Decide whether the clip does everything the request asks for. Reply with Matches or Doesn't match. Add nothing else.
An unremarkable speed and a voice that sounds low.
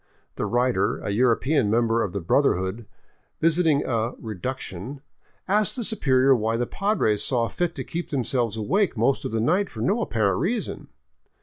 Matches